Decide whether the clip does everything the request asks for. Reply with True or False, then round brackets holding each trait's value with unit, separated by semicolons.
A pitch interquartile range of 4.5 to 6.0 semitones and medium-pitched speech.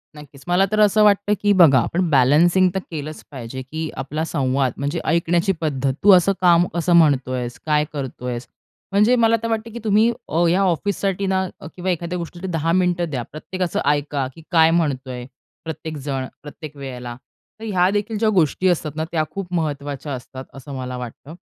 True (5.1 semitones; 160 Hz)